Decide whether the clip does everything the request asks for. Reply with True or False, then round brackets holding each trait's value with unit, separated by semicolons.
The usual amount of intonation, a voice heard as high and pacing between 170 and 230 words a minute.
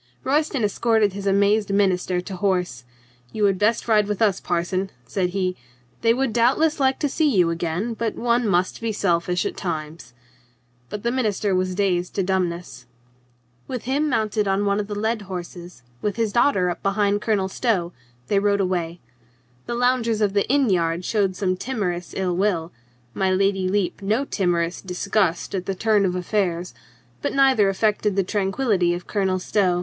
True (3.3 semitones; 195 Hz; 175 wpm)